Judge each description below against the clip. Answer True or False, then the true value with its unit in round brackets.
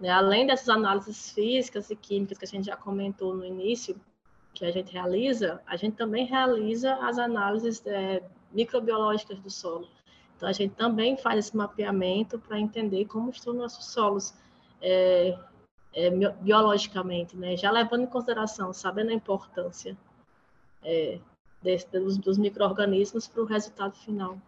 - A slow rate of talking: False (145 wpm)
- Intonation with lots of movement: False (3.0 semitones)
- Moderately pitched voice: False (205 Hz)